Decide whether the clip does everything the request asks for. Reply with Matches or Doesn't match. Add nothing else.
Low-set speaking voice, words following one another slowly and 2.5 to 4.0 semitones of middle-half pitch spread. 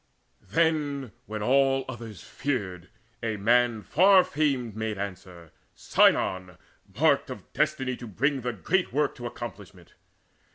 Doesn't match